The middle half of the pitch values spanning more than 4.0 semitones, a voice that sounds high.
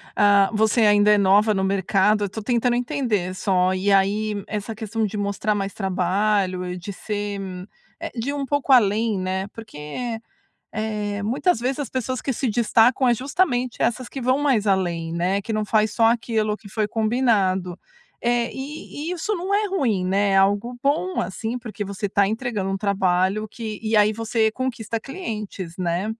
No: average, 3.5 semitones; high, 215 Hz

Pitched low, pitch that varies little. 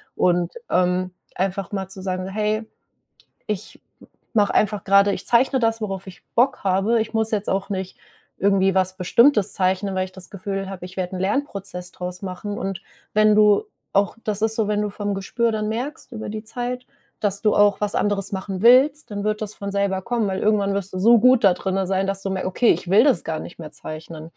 No: high, 200 Hz; narrow, 2.3 semitones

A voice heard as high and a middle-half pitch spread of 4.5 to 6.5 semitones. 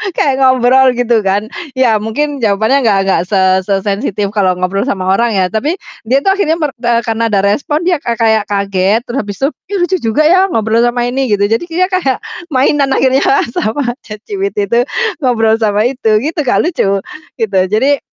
Yes: high, 235 Hz; average, 5.0 semitones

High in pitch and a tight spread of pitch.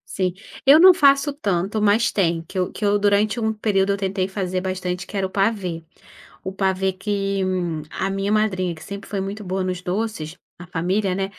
Yes: high, 195 Hz; narrow, 2.1 semitones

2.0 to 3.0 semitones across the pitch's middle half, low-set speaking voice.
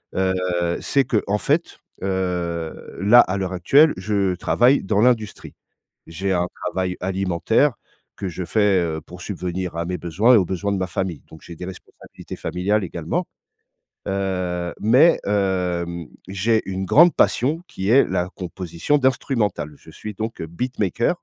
No: average, 3.5 semitones; very low, 95 Hz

